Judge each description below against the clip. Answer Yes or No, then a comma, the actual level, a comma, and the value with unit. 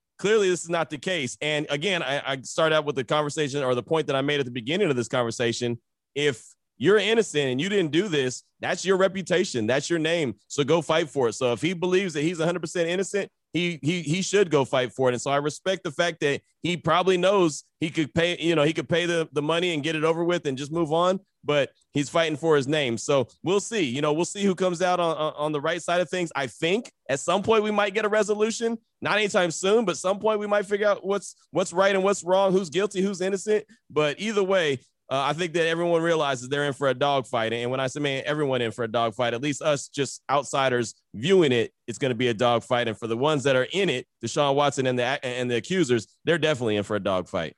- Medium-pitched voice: Yes, medium, 160 Hz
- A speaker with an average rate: No, fast, 255 wpm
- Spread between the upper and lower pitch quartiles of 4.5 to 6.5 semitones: Yes, average, 5.0 semitones